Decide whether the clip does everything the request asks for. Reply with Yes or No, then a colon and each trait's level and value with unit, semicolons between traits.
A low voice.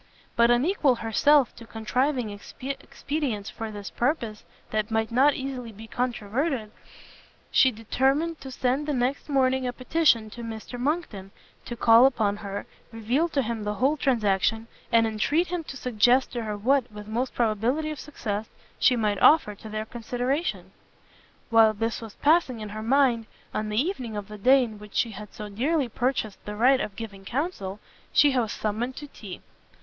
No: high, 235 Hz